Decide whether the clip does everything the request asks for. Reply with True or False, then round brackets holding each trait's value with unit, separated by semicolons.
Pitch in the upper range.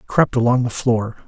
False (120 Hz)